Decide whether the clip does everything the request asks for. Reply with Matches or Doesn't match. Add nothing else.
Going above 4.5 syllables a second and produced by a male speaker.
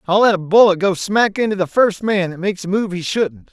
Matches